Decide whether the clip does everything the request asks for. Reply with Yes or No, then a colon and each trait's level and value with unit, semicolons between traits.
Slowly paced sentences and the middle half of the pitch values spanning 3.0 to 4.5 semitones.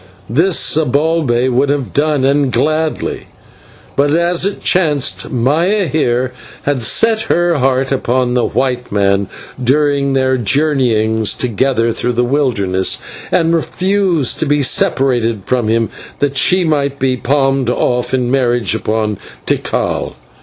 Yes: slow, 130 wpm; average, 3.5 semitones